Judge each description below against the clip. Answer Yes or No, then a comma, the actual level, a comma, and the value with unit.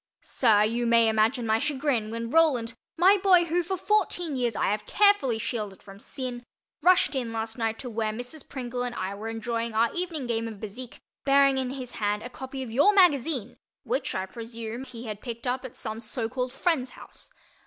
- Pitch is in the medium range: No, high, 245 Hz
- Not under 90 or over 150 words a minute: No, average, 195 wpm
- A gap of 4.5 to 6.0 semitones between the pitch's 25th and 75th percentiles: No, average, 3.7 semitones